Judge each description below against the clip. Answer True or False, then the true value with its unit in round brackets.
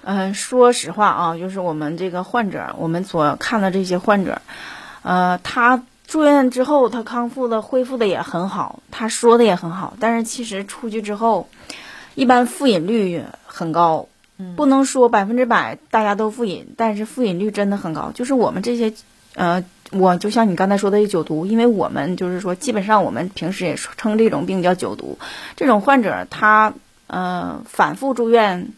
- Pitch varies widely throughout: False (4.6 semitones)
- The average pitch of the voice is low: False (215 Hz)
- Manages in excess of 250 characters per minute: True (275 characters per minute)